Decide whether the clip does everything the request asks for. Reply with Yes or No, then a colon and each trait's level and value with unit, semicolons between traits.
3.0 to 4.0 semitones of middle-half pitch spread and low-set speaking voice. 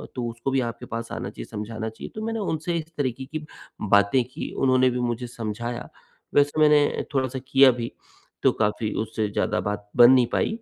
Yes: average, 3.4 semitones; low, 125 Hz